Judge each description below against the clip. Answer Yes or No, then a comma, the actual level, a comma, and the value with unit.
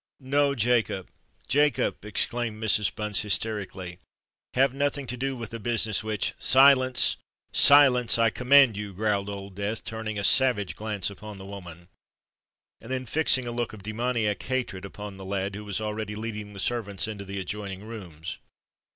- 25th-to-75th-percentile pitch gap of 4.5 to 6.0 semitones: No, average, 3.5 semitones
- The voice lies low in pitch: Yes, low, 110 Hz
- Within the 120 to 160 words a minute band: Yes, average, 155 wpm